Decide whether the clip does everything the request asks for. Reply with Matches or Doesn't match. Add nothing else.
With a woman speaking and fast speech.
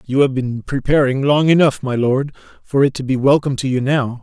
Doesn't match